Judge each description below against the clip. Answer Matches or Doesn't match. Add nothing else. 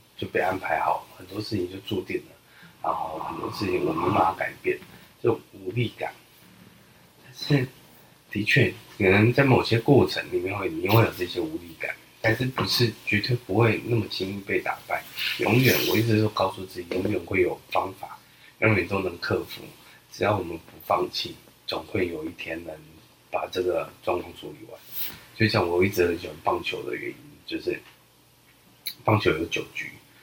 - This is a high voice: Doesn't match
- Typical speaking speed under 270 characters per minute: Matches